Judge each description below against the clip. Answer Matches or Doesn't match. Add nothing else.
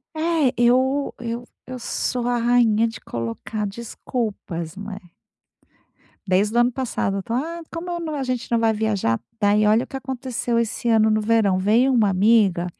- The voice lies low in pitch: Doesn't match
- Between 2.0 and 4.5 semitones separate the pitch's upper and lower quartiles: Matches